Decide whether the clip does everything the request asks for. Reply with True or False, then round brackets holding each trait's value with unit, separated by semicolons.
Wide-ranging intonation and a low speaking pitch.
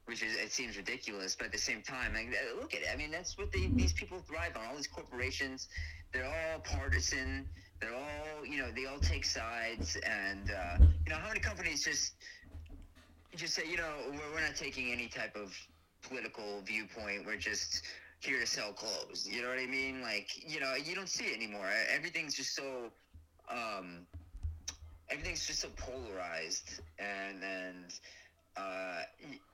True (5.8 semitones; 90 Hz)